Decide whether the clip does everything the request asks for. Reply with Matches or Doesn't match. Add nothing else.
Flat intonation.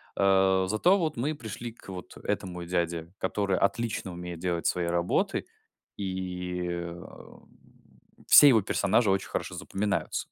Doesn't match